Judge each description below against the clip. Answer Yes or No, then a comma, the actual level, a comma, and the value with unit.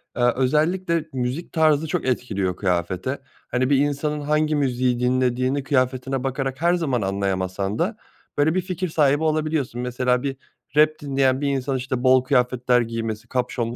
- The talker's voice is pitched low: Yes, low, 130 Hz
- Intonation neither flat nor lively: Yes, average, 3.4 semitones